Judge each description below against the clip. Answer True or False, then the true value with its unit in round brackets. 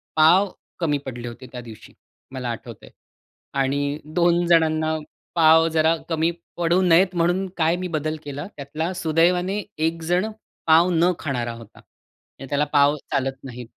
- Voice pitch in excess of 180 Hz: False (160 Hz)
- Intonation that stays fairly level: False (3.6 semitones)